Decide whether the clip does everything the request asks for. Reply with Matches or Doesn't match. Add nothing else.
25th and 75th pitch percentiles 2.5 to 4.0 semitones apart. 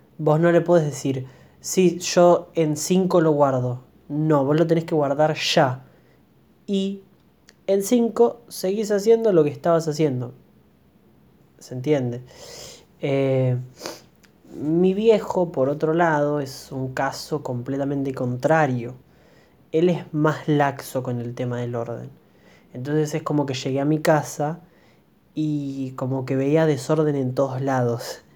Doesn't match